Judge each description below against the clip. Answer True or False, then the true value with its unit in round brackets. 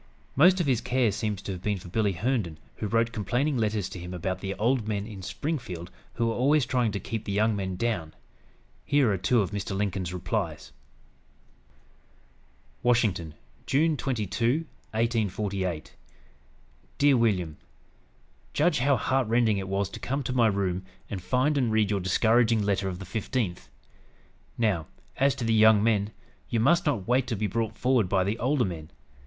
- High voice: False (110 Hz)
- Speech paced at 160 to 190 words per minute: True (175 wpm)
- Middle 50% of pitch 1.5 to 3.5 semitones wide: False (4.2 semitones)